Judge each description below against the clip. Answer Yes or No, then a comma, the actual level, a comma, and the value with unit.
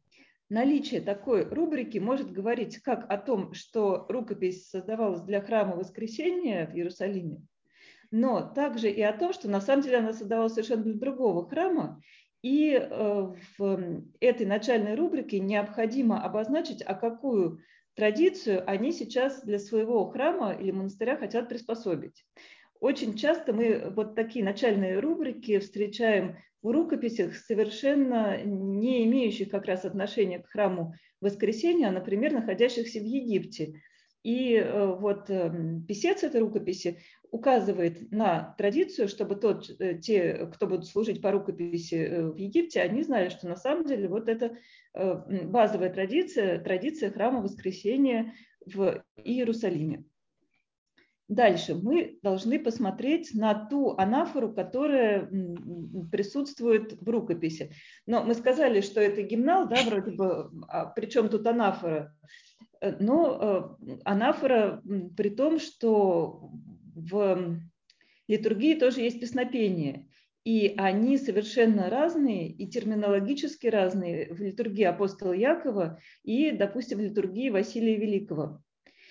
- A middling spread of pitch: Yes, average, 4.3 semitones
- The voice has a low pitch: No, high, 215 Hz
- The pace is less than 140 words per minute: Yes, average, 120 wpm